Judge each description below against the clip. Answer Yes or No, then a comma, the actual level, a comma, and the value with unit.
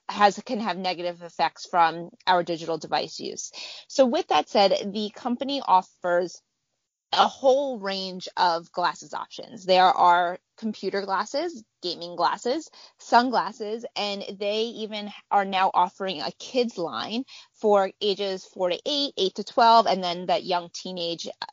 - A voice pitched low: No, high, 195 Hz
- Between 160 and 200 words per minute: No, average, 145 wpm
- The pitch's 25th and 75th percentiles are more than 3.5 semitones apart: Yes, average, 4.4 semitones